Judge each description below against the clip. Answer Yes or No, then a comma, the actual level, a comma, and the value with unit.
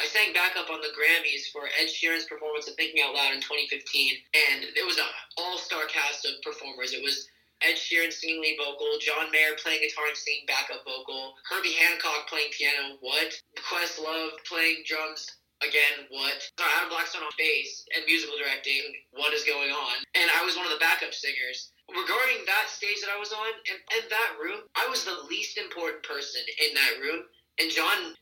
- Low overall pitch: No, medium, 165 Hz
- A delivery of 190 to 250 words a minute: Yes, average, 195 wpm